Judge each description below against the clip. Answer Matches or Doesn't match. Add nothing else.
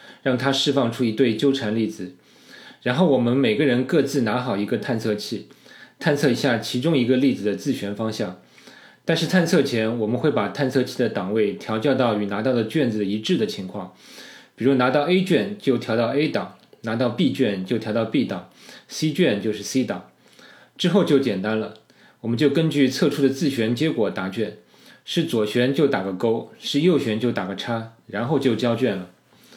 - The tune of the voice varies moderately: Matches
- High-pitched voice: Doesn't match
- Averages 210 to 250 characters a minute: Doesn't match